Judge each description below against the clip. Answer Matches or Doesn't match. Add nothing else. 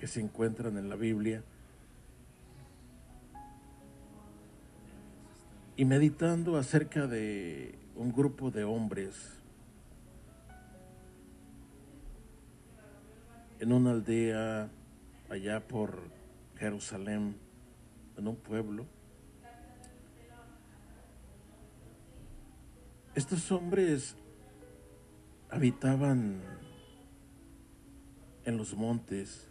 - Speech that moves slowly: Matches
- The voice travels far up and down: Matches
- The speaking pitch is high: Doesn't match